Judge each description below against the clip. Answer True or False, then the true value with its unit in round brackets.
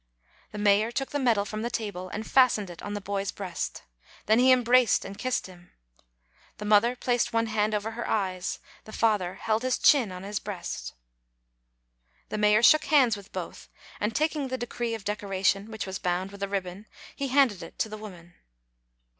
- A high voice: True (215 Hz)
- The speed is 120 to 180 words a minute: False (190 wpm)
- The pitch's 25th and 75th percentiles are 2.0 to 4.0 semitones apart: True (3.3 semitones)